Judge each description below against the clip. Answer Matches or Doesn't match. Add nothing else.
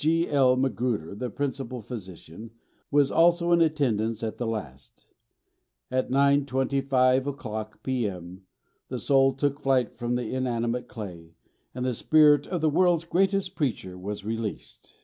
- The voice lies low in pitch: Matches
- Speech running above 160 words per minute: Doesn't match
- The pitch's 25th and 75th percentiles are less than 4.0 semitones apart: Doesn't match